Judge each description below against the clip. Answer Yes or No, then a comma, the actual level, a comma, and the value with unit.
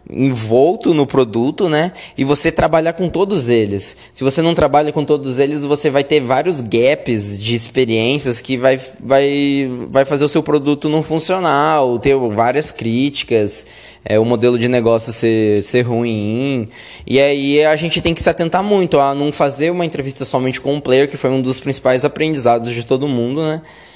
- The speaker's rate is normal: No, fast, 190 wpm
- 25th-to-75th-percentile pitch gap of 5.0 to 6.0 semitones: No, average, 3.8 semitones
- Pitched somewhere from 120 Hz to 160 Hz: Yes, low, 135 Hz